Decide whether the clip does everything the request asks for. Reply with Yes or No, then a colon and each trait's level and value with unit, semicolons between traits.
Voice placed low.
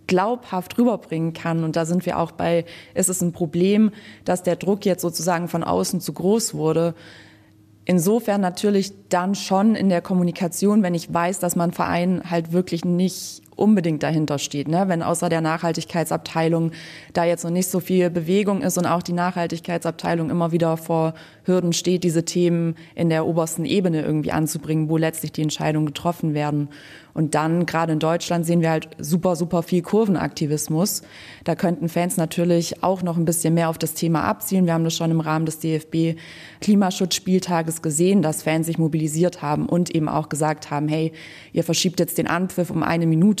No: medium, 170 Hz